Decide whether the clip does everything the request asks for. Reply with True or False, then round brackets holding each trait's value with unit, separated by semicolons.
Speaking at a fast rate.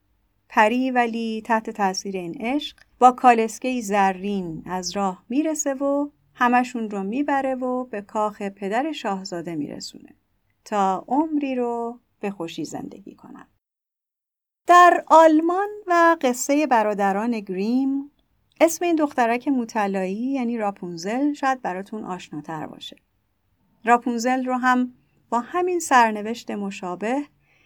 False (115 wpm)